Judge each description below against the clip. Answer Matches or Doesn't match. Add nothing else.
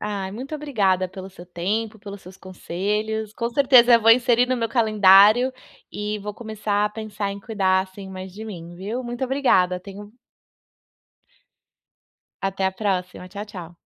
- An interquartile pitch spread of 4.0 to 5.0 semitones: Doesn't match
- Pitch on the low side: Doesn't match